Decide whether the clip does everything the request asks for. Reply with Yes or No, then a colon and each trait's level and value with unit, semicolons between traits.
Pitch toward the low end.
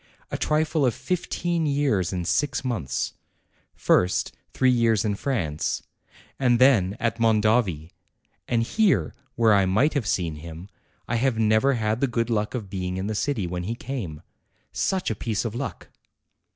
Yes: low, 115 Hz